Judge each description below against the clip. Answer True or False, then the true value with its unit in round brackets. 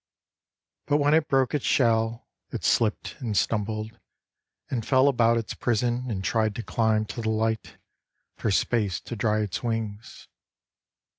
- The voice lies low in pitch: True (115 Hz)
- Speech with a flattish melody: True (2.0 semitones)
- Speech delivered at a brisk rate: False (150 wpm)